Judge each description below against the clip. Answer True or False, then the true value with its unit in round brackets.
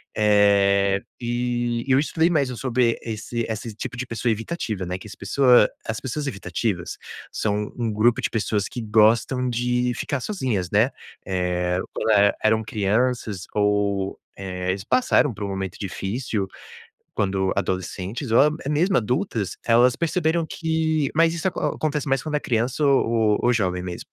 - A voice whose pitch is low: True (115 Hz)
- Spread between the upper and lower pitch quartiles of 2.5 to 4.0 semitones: False (4.4 semitones)